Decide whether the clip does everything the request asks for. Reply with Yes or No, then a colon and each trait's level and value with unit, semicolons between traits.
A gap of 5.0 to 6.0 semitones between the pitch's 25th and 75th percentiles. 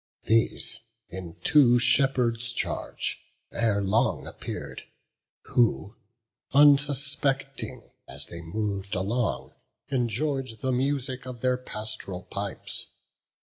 No: average, 3.9 semitones